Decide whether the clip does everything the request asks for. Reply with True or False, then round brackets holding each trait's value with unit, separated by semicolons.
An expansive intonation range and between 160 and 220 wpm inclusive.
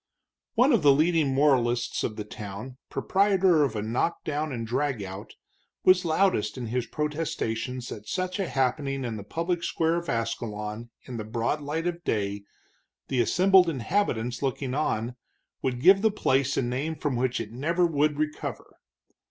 True (5.9 semitones; 170 wpm)